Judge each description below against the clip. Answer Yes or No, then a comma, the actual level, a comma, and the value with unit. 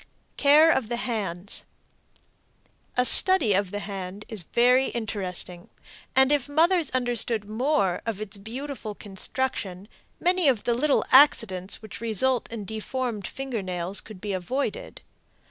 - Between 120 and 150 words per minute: Yes, slow, 135 wpm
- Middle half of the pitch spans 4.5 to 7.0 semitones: Yes, average, 5.0 semitones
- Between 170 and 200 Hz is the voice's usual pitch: No, high, 225 Hz